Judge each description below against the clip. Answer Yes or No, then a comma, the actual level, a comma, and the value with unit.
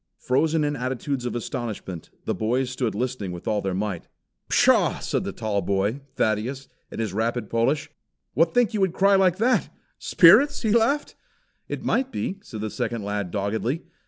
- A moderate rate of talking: Yes, average, 175 wpm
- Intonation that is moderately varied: No, wide, 7.6 semitones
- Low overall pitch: Yes, low, 125 Hz